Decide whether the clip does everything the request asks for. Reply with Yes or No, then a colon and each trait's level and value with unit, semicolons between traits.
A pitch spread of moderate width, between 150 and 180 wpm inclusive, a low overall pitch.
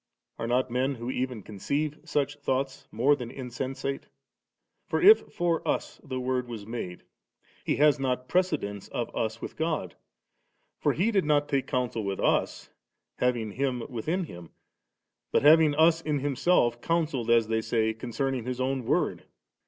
Yes: average, 4.0 semitones; average, 165 wpm; low, 130 Hz